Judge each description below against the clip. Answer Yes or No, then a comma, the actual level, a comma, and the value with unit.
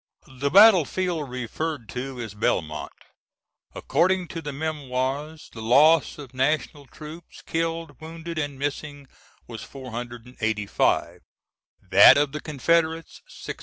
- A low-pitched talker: No, medium, 145 Hz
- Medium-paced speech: No, slow, 120 wpm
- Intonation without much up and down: No, average, 4.2 semitones